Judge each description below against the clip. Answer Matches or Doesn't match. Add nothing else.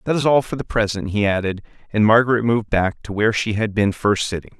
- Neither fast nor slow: Doesn't match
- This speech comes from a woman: Doesn't match